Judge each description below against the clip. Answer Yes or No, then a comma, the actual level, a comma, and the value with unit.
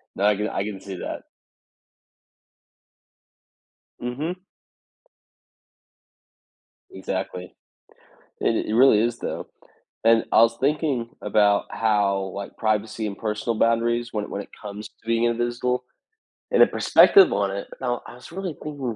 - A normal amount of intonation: Yes, average, 3.0 semitones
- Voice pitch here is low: Yes, low, 115 Hz